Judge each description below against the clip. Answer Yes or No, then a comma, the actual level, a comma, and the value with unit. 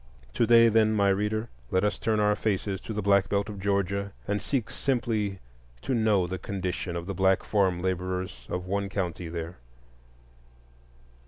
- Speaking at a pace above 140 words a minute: Yes, average, 170 wpm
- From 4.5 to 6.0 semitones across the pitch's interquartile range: No, narrow, 2.4 semitones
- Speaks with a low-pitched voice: Yes, low, 100 Hz